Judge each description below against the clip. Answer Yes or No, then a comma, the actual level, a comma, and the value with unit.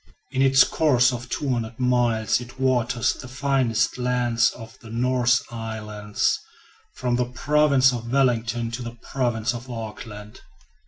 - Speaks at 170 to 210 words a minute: No, average, 140 wpm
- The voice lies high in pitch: No, low, 120 Hz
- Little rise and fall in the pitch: Yes, narrow, 1.9 semitones